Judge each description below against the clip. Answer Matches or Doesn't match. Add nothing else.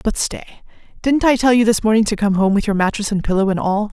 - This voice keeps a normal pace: Doesn't match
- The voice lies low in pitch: Doesn't match